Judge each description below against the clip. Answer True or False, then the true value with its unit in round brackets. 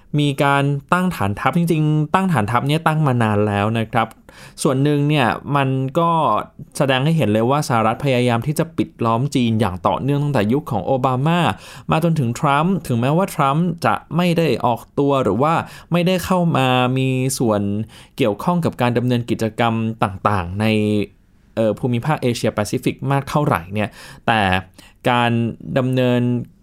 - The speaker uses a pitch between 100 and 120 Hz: False (130 Hz)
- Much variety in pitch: False (4.9 semitones)